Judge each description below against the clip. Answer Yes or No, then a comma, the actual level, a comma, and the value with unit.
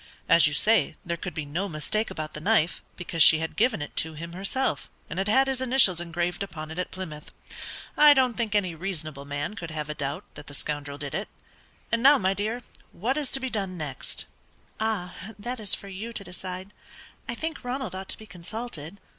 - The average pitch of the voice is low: No, medium, 185 Hz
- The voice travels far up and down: Yes, wide, 5.8 semitones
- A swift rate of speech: Yes, fast, 215 wpm